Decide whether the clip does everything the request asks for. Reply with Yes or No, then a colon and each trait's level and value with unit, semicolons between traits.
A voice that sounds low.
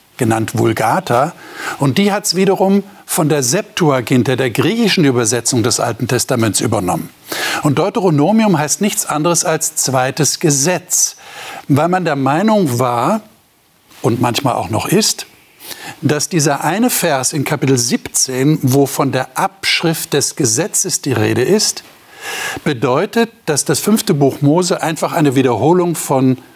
No: medium, 155 Hz